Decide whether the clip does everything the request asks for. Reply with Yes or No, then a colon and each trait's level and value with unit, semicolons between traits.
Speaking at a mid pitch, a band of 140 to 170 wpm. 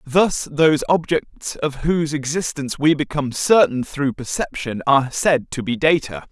Yes: medium, 145 Hz; average, 150 wpm